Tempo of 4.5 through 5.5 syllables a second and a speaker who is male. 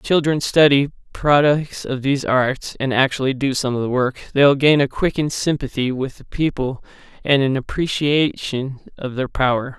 Yes: 4.9 syllables/s; male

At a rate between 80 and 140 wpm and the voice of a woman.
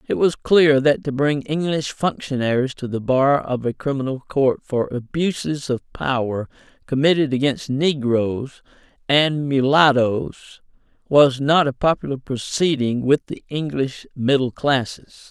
No: slow, 135 wpm; male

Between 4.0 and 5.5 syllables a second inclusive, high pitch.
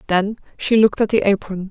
No: 6.1 syllables/s; high, 205 Hz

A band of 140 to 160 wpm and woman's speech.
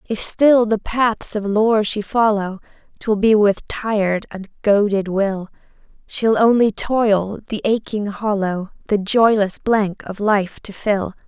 Yes: average, 150 wpm; female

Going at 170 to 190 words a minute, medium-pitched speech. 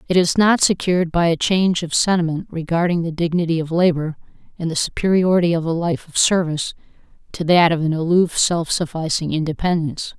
Yes: average, 175 wpm; medium, 170 Hz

